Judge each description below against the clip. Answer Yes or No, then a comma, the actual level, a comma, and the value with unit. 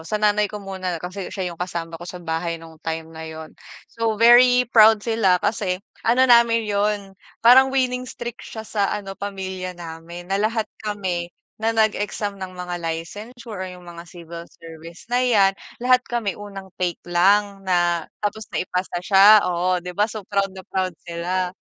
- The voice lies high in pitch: Yes, high, 195 Hz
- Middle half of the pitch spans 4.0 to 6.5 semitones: No, average, 3.6 semitones